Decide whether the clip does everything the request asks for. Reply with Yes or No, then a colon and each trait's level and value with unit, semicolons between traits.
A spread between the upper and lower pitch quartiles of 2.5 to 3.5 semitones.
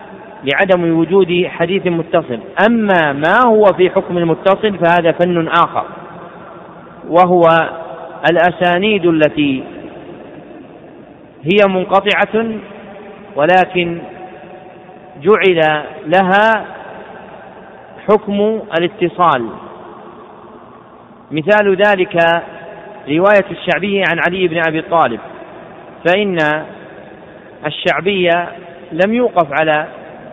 Yes: average, 3.0 semitones